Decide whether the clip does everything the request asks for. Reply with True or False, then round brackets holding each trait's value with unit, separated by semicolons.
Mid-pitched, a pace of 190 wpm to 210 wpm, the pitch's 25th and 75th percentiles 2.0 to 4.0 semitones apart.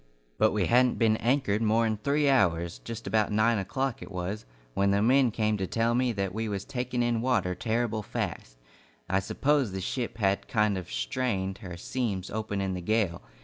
False (110 Hz; 195 wpm; 3.7 semitones)